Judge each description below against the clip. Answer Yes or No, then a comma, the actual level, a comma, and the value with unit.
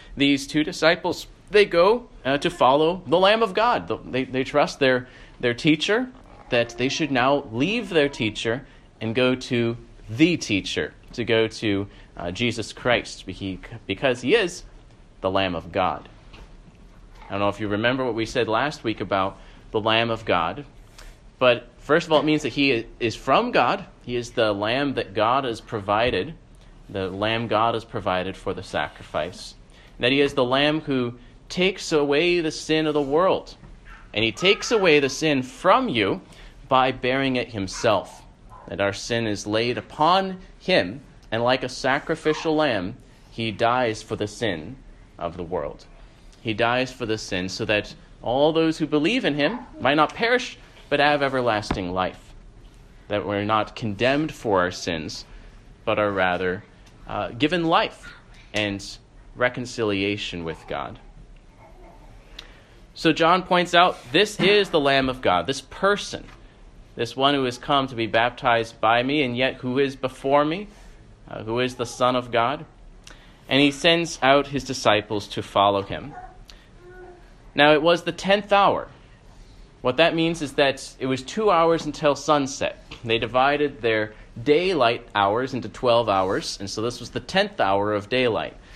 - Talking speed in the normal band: Yes, average, 165 wpm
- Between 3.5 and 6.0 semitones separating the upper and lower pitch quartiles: Yes, wide, 5.4 semitones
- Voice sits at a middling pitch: No, low, 125 Hz